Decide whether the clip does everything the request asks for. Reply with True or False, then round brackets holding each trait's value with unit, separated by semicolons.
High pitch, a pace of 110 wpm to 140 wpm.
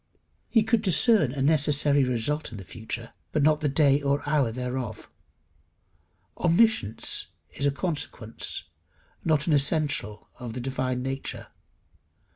False (140 Hz; 135 wpm)